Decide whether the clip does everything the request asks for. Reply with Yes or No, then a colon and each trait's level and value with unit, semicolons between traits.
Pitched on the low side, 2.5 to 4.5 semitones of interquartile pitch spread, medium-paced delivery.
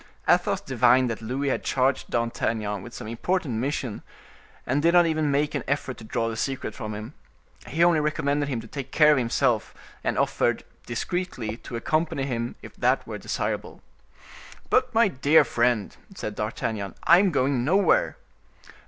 No: low, 130 Hz; average, 4.9 semitones; average, 170 wpm